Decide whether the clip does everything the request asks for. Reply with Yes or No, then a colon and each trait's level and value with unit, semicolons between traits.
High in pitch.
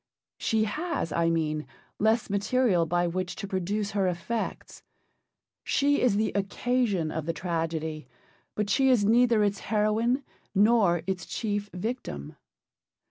Yes: high, 200 Hz